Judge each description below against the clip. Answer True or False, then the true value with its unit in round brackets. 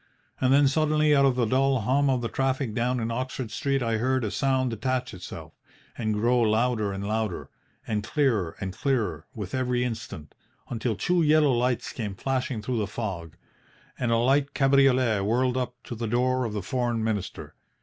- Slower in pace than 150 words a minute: False (185 wpm)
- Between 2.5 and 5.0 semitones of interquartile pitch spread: True (3.2 semitones)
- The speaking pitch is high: False (125 Hz)